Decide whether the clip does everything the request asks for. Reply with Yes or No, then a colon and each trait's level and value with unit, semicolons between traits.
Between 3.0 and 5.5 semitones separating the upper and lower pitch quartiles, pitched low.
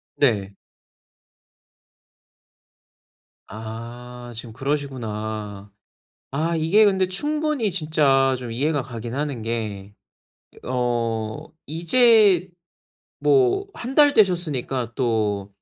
No: wide, 7.8 semitones; low, 130 Hz